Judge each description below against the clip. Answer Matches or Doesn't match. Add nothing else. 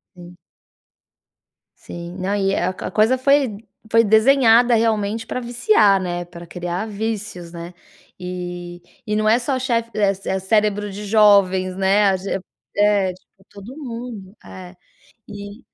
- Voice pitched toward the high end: Matches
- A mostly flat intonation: Doesn't match